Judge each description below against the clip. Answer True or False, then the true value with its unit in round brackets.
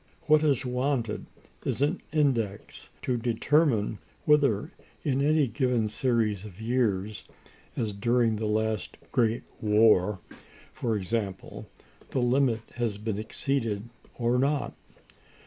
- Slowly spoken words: True (115 wpm)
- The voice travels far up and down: False (3.9 semitones)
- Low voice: True (115 Hz)